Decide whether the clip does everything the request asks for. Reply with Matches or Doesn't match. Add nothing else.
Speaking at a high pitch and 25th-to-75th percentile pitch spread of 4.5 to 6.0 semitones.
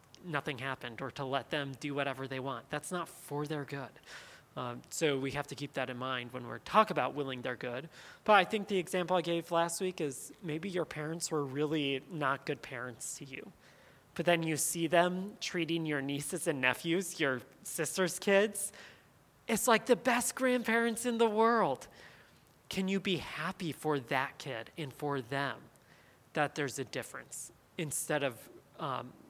Doesn't match